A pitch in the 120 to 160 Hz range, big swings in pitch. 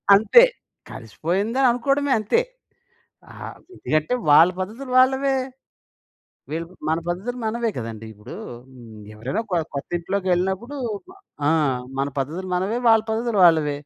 No: high, 190 Hz; wide, 7.5 semitones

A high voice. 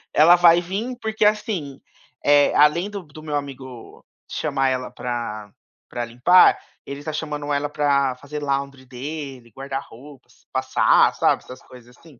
No: medium, 145 Hz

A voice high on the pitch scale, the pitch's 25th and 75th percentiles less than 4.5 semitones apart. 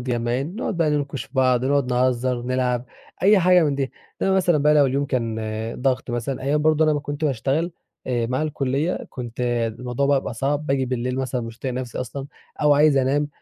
No: low, 135 Hz; average, 2.8 semitones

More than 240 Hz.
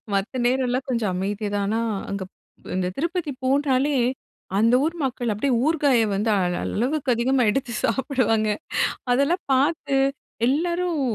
Yes: very high, 255 Hz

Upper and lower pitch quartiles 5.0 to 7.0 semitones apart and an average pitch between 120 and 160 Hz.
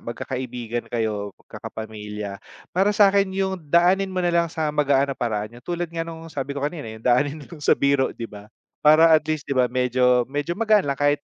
Yes: wide, 5.6 semitones; medium, 140 Hz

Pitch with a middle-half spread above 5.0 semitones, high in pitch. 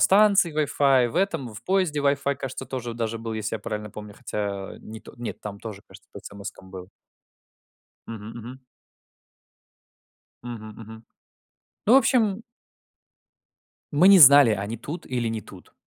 No: wide, 5.4 semitones; low, 120 Hz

